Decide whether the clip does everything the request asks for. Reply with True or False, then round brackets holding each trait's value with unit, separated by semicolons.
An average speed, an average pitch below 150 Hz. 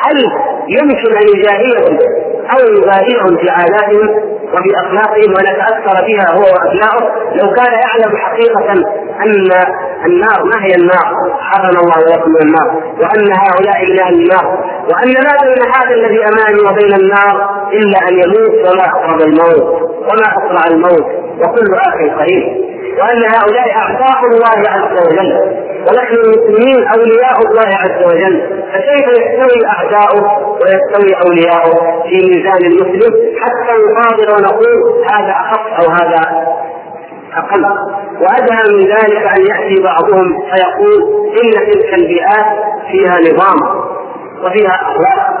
False (125 wpm; 215 Hz)